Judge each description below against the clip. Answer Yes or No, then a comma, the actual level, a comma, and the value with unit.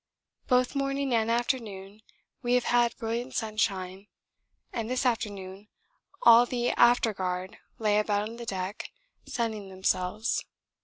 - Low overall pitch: No, high, 225 Hz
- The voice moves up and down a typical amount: Yes, average, 3.5 semitones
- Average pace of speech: No, slow, 125 wpm